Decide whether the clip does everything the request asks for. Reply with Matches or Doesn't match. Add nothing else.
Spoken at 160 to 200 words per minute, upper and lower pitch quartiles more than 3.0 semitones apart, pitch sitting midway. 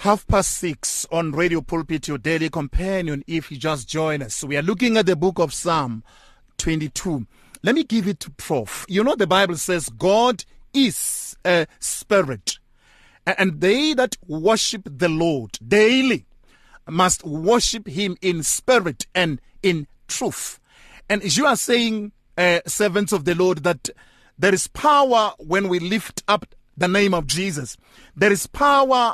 Matches